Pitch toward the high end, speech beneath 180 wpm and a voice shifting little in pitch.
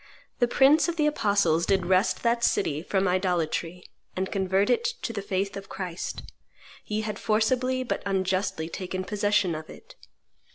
No: high, 195 Hz; average, 160 wpm; average, 3.0 semitones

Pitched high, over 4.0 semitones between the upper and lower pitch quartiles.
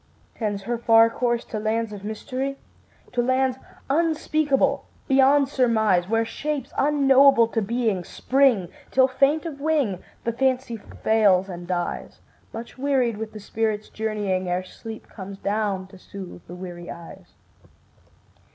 Yes: high, 225 Hz; average, 5.0 semitones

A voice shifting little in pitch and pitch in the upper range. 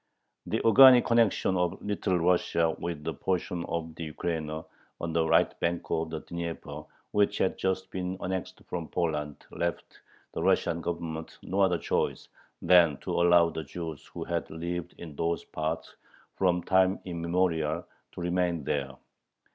No: narrow, 2.1 semitones; very low, 85 Hz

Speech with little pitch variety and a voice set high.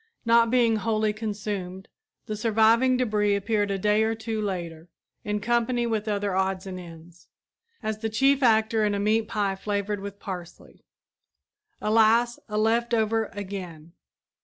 Yes: narrow, 2.2 semitones; high, 215 Hz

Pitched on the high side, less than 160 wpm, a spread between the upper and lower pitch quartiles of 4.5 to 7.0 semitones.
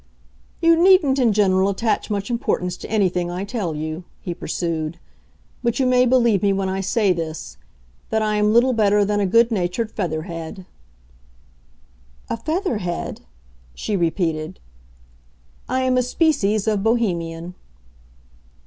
Yes: high, 200 Hz; average, 140 wpm; average, 5.1 semitones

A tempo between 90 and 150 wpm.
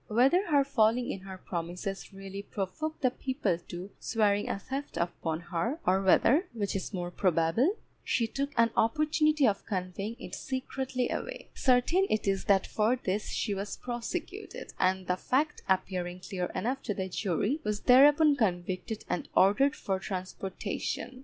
No: average, 160 wpm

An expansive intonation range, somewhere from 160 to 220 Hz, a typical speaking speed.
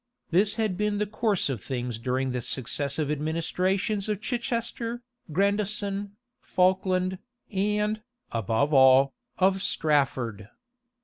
No: wide, 7.4 semitones; medium, 185 Hz; slow, 115 wpm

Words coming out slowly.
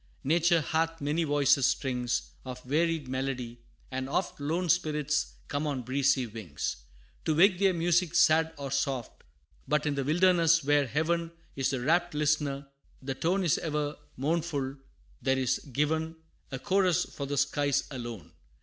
No: average, 150 wpm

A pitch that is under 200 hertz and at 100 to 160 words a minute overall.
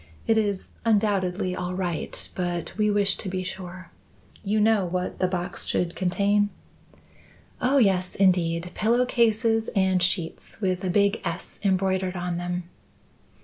Yes: high, 190 Hz; average, 145 wpm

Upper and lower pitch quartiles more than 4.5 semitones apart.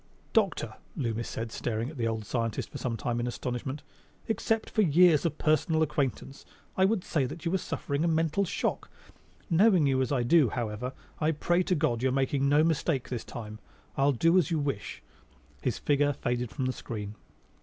Yes: average, 5.1 semitones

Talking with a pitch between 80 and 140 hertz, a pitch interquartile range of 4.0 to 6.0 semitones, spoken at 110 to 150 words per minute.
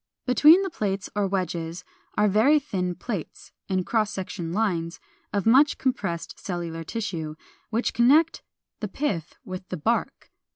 No: high, 200 Hz; average, 5.2 semitones; average, 140 wpm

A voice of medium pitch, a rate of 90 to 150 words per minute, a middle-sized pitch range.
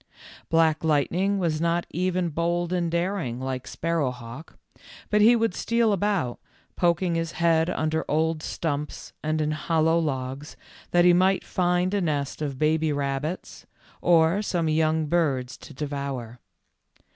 Yes: medium, 160 Hz; average, 145 wpm; average, 3.0 semitones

